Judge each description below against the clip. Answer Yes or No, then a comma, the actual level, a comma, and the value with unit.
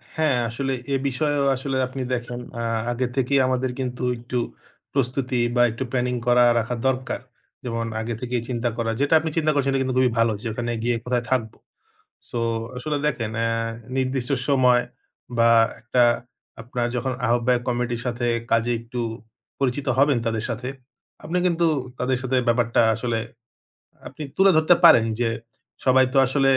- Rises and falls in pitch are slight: Yes, narrow, 2.1 semitones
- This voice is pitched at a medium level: No, low, 125 Hz